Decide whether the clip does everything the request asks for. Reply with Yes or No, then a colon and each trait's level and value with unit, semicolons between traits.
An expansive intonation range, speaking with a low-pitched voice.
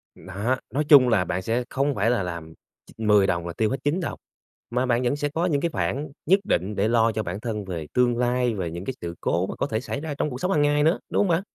Yes: wide, 6.7 semitones; low, 120 Hz